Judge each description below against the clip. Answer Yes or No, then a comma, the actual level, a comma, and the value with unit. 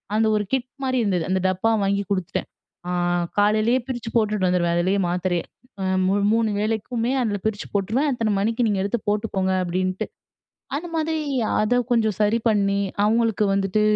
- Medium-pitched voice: No, high, 210 Hz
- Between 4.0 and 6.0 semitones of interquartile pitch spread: No, average, 3.0 semitones